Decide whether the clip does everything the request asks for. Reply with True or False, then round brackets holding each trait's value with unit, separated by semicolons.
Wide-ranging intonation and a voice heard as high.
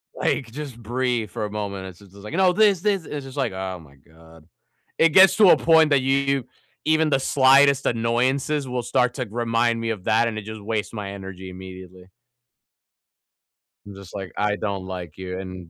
False (6.2 semitones; 115 Hz)